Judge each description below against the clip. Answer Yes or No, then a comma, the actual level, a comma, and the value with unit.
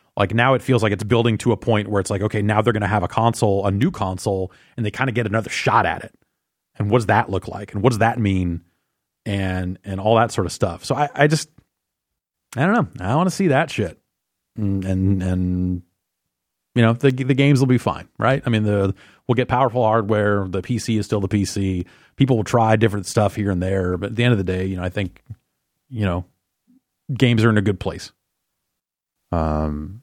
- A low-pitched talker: Yes, low, 105 Hz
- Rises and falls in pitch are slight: No, average, 4.1 semitones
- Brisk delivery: Yes, fast, 235 wpm